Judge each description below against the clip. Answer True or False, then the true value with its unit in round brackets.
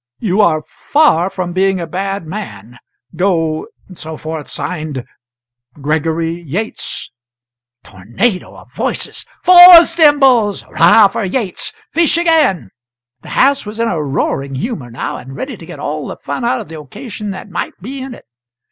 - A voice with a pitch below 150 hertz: False (185 Hz)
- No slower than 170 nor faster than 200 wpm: False (150 wpm)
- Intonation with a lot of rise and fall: True (7.1 semitones)